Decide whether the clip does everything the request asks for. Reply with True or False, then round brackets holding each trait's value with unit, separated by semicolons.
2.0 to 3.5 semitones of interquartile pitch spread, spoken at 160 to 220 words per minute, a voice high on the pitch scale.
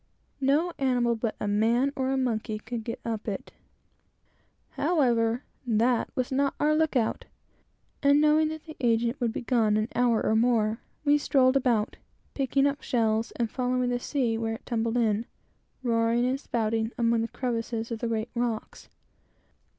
True (2.7 semitones; 165 wpm; 240 Hz)